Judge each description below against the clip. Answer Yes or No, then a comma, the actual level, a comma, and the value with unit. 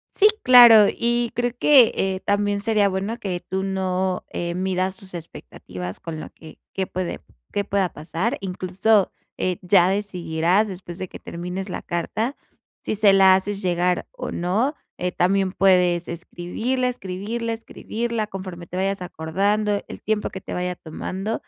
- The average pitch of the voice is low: No, high, 190 Hz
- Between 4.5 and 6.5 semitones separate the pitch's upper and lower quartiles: No, average, 2.8 semitones